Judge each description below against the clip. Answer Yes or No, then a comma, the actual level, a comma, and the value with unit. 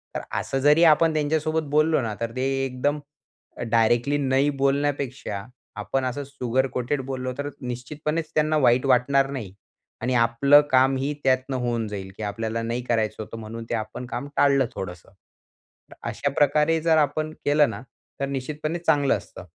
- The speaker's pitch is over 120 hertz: Yes, low, 135 Hz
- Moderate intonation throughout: Yes, average, 3.4 semitones